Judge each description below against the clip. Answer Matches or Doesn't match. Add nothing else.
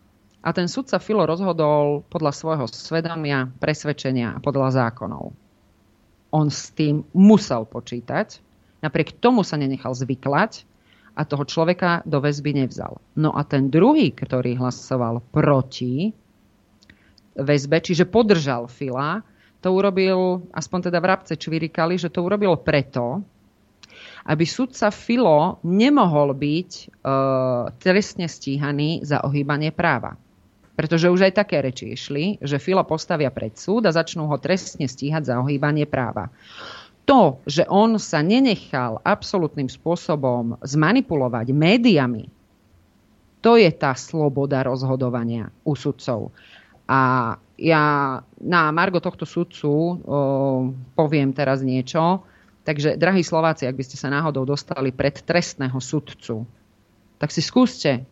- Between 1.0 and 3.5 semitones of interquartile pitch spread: Doesn't match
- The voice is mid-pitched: Matches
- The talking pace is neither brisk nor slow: Matches